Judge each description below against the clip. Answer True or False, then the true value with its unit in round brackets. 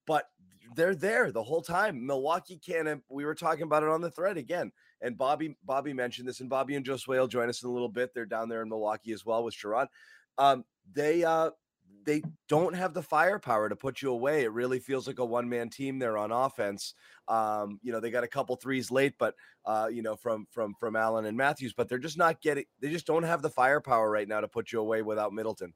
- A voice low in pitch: True (125 Hz)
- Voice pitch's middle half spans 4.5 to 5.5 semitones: True (5.2 semitones)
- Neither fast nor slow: False (240 wpm)